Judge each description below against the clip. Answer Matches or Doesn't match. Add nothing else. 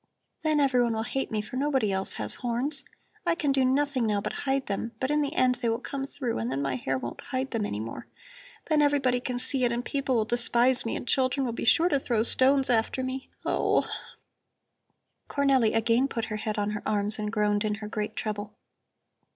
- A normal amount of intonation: Matches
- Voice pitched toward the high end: Matches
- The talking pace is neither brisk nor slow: Doesn't match